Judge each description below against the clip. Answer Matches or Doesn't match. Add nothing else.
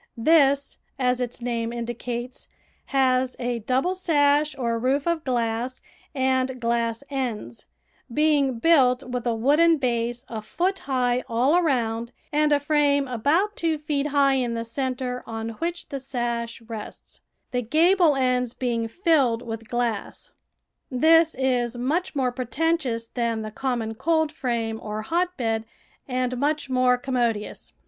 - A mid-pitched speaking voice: Doesn't match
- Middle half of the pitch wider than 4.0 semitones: Doesn't match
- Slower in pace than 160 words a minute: Matches